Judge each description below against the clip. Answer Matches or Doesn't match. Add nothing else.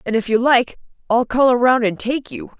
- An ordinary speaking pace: Doesn't match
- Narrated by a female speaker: Matches